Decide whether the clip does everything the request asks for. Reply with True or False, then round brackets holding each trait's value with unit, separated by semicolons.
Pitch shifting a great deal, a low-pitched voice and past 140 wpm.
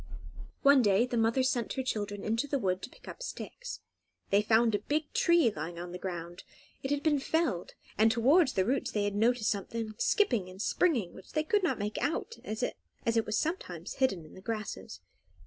False (5.8 semitones; 225 Hz; 200 wpm)